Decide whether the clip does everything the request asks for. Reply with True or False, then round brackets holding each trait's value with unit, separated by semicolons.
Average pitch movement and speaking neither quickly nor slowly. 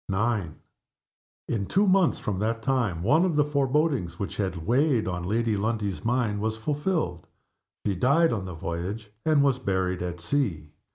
False (7.1 semitones; 165 wpm)